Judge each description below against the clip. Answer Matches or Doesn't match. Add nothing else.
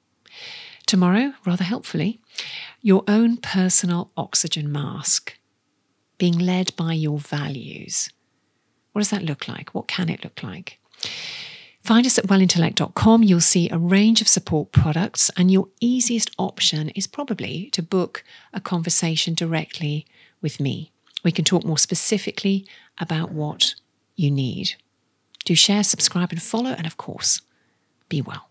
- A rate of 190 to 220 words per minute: Doesn't match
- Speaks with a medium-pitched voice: Matches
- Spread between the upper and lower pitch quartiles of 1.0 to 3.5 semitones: Doesn't match